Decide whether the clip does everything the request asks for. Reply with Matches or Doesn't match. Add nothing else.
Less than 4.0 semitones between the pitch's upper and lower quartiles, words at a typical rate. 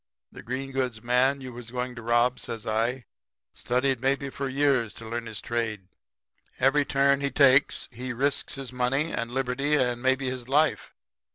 Matches